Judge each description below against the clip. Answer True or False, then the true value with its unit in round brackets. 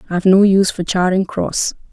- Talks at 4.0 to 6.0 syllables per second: True (5.7 syllables/s)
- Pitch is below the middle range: False (185 Hz)